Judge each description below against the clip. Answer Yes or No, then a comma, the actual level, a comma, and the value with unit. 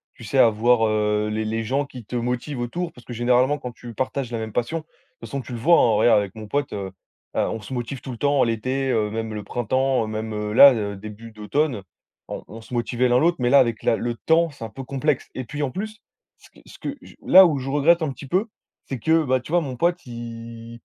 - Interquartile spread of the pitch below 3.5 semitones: No, average, 3.9 semitones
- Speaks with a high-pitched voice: No, low, 120 Hz